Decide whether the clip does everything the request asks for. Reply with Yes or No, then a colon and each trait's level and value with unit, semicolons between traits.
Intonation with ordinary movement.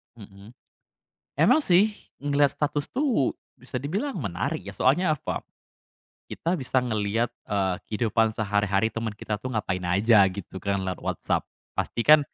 No: wide, 6.2 semitones